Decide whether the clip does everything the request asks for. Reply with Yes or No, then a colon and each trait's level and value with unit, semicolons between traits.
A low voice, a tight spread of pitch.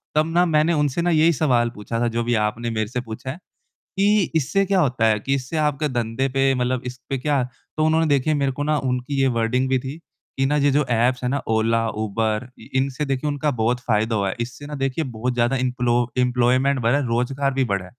No: low, 130 Hz; average, 3.4 semitones